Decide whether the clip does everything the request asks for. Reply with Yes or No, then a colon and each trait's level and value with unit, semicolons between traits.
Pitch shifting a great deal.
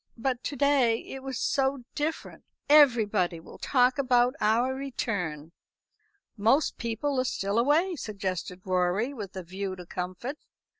Yes: wide, 6.1 semitones